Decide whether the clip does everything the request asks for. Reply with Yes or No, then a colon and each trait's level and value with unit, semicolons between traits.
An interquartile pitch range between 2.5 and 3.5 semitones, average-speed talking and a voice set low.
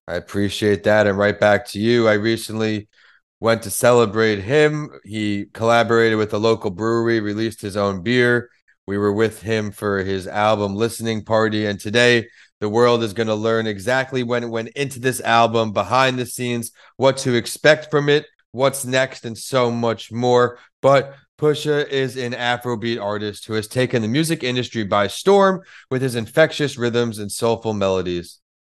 Yes: average, 2.8 semitones; average, 175 wpm; low, 115 Hz